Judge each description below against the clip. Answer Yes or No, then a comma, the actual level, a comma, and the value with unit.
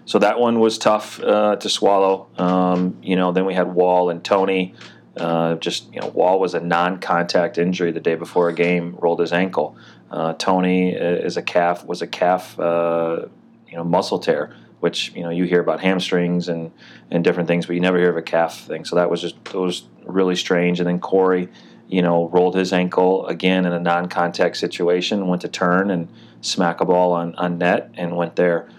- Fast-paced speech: Yes, fast, 210 wpm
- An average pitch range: No, narrow, 1.2 semitones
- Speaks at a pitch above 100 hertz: No, very low, 90 Hz